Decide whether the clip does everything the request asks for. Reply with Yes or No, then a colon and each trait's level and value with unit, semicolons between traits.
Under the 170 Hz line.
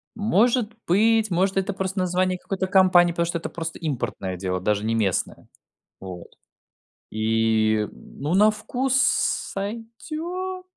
No: medium, 185 Hz